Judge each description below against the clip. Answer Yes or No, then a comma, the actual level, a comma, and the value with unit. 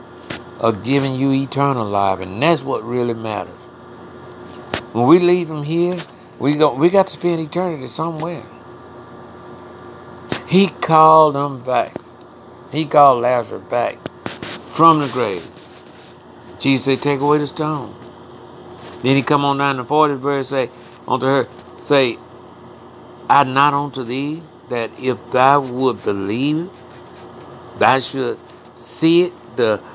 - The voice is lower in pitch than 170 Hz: Yes, low, 135 Hz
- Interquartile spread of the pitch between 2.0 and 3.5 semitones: No, average, 4.1 semitones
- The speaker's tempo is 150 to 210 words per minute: No, slow, 135 wpm